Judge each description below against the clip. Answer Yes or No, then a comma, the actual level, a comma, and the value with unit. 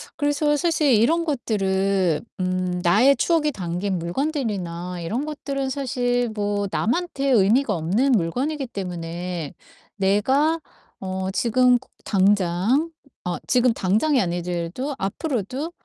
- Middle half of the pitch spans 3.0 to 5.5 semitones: No, wide, 7.1 semitones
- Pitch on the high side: Yes, high, 215 Hz